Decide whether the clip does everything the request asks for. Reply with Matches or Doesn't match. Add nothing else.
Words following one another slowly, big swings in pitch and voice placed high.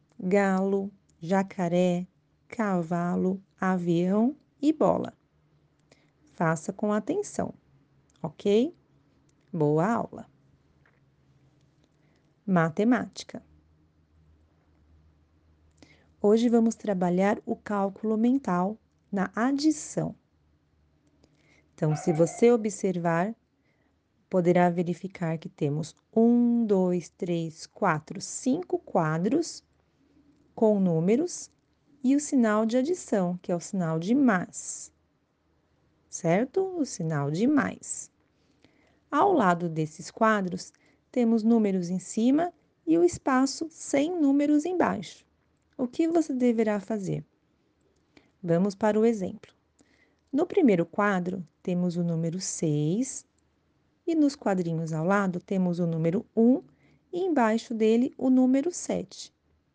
Matches